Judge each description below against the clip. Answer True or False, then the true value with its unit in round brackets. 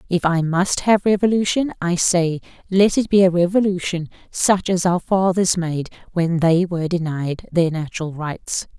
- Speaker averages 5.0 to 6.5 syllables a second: False (4.6 syllables/s)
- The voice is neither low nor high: True (175 Hz)